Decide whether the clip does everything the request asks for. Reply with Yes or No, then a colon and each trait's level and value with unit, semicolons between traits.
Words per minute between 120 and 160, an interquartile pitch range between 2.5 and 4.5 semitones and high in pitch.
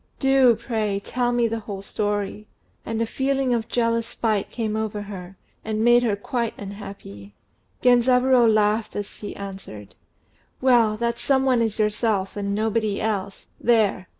Yes: average, 150 wpm; average, 2.8 semitones; high, 220 Hz